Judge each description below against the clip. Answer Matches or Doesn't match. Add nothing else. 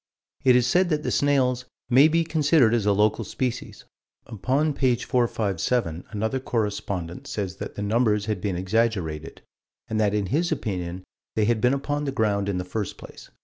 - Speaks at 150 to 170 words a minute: Doesn't match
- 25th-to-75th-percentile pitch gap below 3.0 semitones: Doesn't match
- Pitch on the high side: Doesn't match